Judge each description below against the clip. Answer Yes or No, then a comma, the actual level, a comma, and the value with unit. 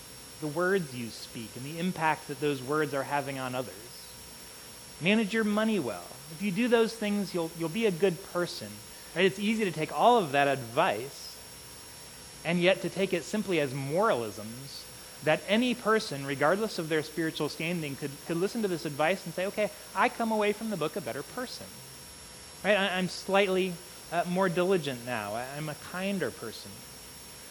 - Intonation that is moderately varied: No, wide, 6.1 semitones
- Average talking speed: Yes, average, 185 wpm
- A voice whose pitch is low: No, medium, 170 Hz